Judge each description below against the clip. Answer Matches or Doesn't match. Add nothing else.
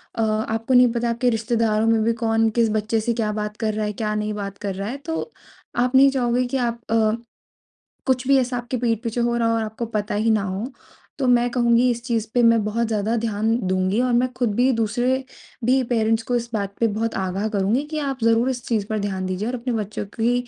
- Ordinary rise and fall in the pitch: Doesn't match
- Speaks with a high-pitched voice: Matches